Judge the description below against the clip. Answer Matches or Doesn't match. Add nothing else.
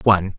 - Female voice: Doesn't match